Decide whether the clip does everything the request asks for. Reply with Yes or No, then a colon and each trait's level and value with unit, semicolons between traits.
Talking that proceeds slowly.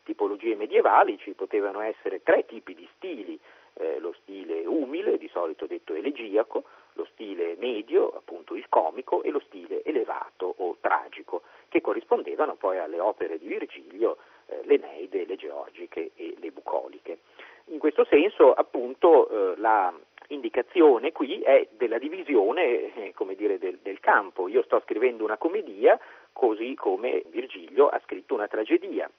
No: average, 145 wpm